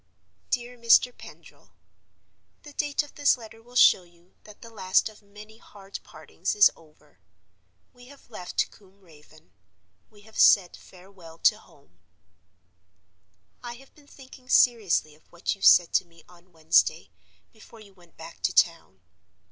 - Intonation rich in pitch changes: Yes, wide, 5.7 semitones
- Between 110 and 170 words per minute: Yes, average, 155 wpm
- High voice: Yes, high, 200 Hz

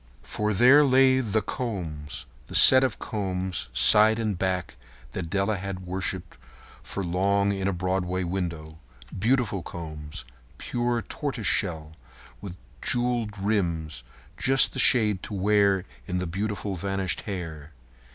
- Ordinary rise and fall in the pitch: Yes, average, 3.4 semitones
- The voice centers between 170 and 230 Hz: No, very low, 95 Hz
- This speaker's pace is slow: Yes, slow, 120 wpm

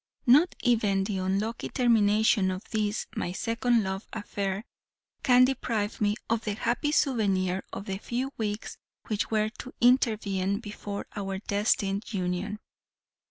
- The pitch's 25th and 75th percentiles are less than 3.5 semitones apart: Yes, average, 2.9 semitones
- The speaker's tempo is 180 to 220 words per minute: No, slow, 135 wpm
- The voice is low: No, high, 210 Hz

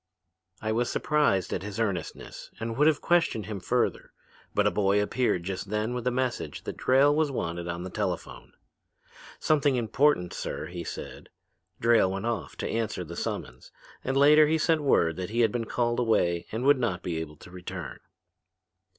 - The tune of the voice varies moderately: No, wide, 6.3 semitones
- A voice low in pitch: Yes, low, 110 Hz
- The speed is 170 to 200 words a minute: Yes, average, 185 wpm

